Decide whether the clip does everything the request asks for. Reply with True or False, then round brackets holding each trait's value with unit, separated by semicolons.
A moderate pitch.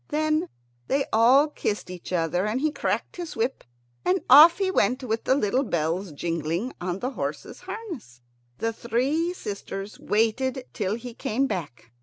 False (230 Hz)